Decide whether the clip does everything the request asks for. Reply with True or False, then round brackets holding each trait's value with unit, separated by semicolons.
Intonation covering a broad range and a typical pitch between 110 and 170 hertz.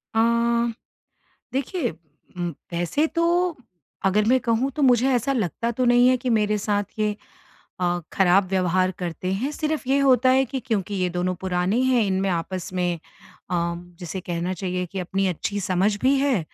False (5.7 semitones; 205 Hz)